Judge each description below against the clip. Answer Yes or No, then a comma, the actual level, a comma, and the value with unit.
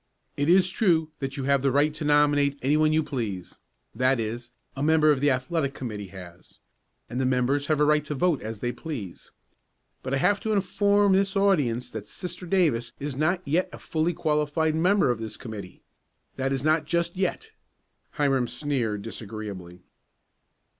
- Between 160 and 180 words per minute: Yes, average, 175 wpm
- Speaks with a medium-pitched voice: Yes, medium, 145 Hz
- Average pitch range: Yes, average, 4.8 semitones